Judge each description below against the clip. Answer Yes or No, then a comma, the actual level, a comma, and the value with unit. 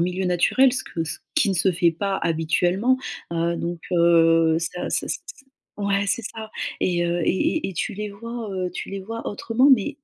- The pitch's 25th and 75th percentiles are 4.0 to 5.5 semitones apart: Yes, average, 4.3 semitones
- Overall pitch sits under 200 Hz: Yes, medium, 185 Hz